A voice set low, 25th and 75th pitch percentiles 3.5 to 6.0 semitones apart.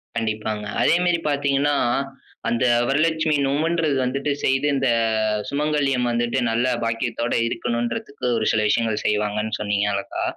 Yes: low, 125 Hz; average, 4.1 semitones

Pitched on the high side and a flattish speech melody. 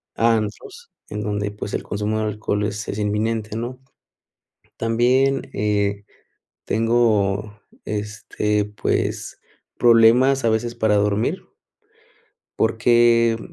No: low, 110 Hz; narrow, 2.0 semitones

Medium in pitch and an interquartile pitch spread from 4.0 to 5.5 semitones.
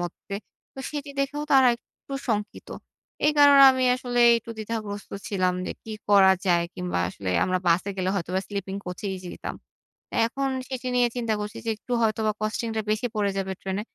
No: high, 215 Hz; average, 4.5 semitones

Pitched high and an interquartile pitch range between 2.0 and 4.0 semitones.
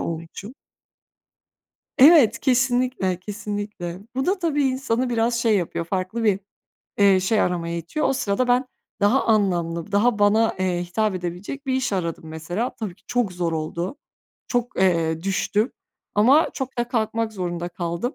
No: high, 205 Hz; wide, 5.6 semitones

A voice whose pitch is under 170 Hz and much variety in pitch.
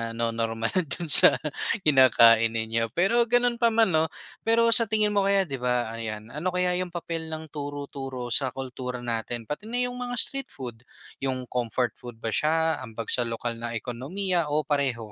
Yes: low, 135 Hz; wide, 7.4 semitones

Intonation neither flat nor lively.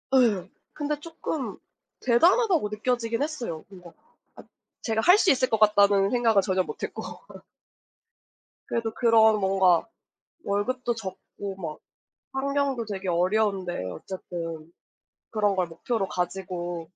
Yes: average, 4.8 semitones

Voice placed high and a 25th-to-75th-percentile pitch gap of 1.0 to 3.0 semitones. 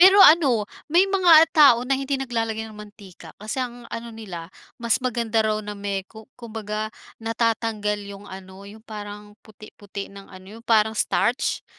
Yes: high, 220 Hz; narrow, 2.6 semitones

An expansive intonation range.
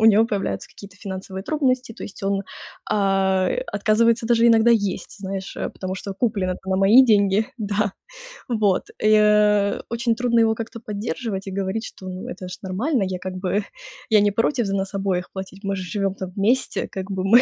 No: average, 2.8 semitones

